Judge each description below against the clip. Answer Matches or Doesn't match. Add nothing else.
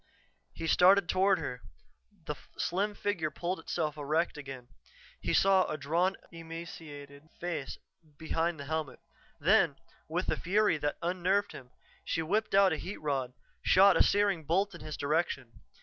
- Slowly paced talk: Doesn't match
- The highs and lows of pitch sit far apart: Doesn't match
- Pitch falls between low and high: Matches